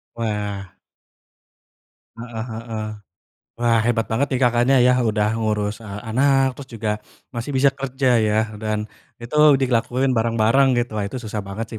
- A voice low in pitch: Yes, low, 115 Hz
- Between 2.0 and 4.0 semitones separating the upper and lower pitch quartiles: Yes, average, 2.7 semitones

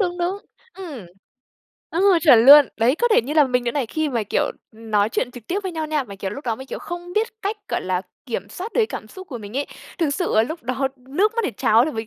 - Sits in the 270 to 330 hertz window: Yes, very high, 280 Hz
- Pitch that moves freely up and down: Yes, wide, 7.5 semitones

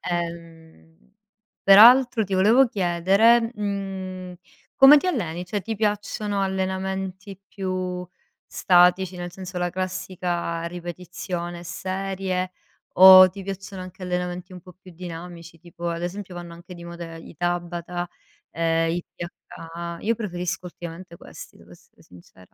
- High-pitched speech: No, medium, 180 Hz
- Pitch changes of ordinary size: No, narrow, 2.0 semitones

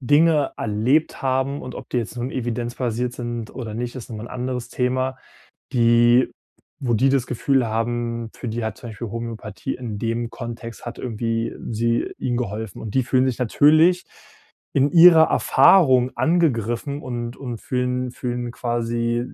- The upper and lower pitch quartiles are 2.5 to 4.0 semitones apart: No, narrow, 1.9 semitones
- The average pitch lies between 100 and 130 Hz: Yes, low, 120 Hz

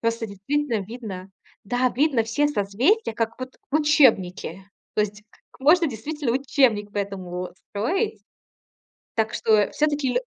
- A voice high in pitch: Yes, high, 230 Hz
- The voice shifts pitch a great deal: Yes, wide, 6.1 semitones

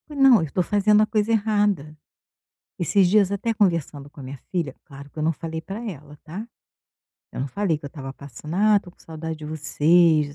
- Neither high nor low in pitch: Yes, medium, 165 Hz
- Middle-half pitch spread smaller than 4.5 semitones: No, wide, 5.5 semitones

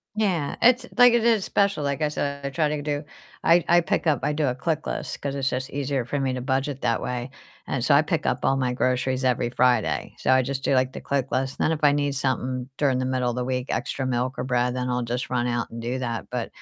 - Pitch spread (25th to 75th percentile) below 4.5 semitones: Yes, narrow, 2.5 semitones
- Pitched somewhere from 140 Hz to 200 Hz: No, low, 130 Hz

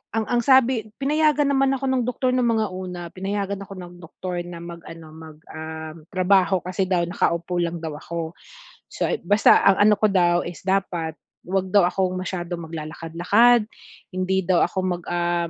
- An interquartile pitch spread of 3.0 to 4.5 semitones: Yes, average, 3.3 semitones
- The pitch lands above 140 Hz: Yes, medium, 185 Hz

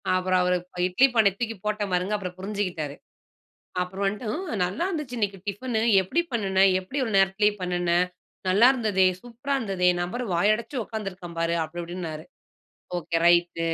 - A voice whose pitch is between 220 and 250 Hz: No, high, 195 Hz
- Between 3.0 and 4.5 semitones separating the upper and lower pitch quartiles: Yes, average, 3.6 semitones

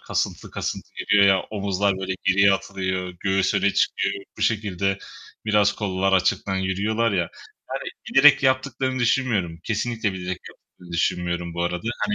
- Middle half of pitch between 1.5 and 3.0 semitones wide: Yes, average, 2.7 semitones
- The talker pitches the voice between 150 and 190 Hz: No, low, 100 Hz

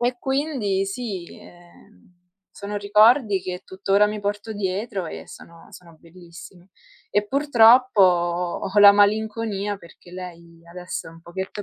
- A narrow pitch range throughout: No, average, 3.3 semitones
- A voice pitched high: Yes, high, 195 Hz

